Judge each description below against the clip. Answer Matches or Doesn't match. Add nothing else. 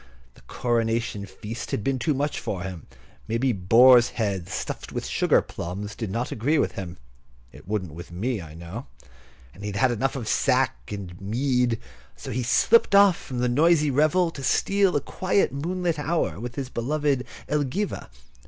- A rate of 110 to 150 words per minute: Doesn't match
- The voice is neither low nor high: Doesn't match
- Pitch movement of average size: Doesn't match